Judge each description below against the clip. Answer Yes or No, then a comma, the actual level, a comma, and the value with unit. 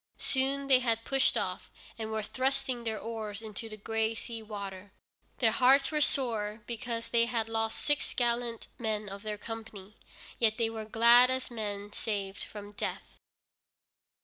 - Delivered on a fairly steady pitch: Yes, narrow, 2.3 semitones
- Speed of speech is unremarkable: Yes, average, 160 wpm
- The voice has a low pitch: No, high, 225 Hz